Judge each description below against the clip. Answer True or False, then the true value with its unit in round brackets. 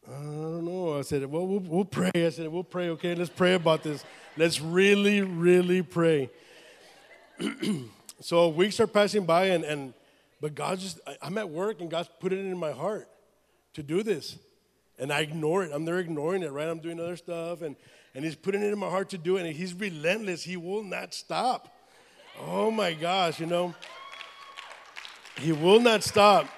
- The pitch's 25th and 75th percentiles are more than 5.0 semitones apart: False (3.0 semitones)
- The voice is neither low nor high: True (175 Hz)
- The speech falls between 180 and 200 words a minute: True (195 wpm)